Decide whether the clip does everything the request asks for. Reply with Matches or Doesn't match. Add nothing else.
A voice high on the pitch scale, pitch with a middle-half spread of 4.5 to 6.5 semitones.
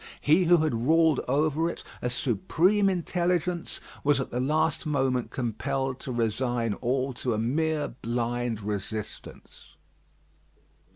Doesn't match